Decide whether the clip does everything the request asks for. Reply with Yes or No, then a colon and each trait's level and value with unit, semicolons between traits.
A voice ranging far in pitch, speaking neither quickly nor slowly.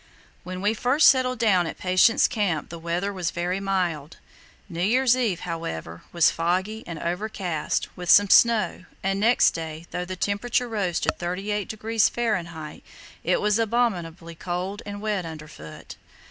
No: average, 4.1 semitones; average, 150 wpm